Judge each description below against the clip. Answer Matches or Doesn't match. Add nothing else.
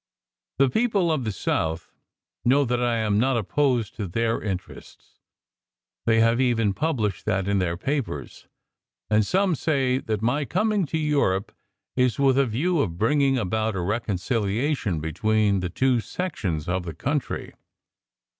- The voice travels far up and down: Matches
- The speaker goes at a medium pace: Matches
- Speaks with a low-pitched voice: Matches